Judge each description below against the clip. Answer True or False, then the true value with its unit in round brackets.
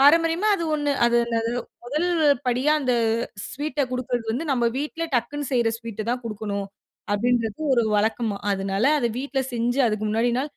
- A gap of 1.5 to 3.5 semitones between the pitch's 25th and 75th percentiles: False (4.0 semitones)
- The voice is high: True (245 Hz)